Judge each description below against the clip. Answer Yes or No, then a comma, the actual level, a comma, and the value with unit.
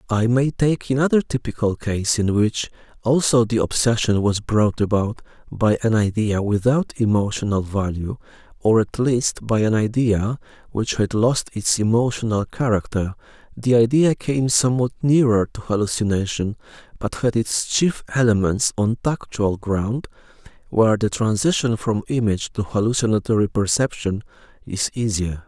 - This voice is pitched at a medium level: No, low, 115 Hz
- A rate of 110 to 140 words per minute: Yes, slow, 135 wpm